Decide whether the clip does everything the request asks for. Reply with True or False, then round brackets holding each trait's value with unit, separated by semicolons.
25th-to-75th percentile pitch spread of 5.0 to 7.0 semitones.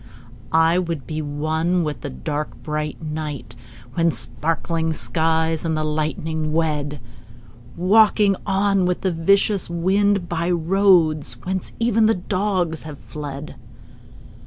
False (3.2 semitones)